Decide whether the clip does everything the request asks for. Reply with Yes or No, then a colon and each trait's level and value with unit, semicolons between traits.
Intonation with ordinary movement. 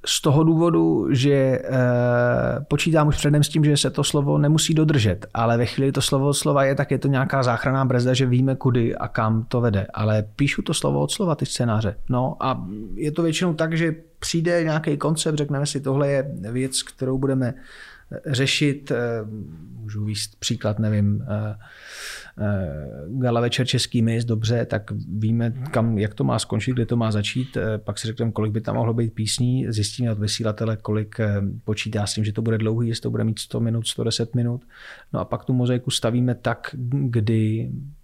Yes: average, 4.0 semitones